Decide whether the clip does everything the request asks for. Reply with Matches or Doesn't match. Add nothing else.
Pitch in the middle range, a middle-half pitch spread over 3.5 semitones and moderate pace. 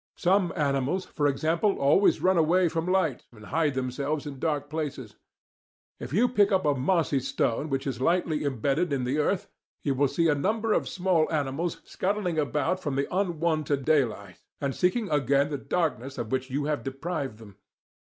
Matches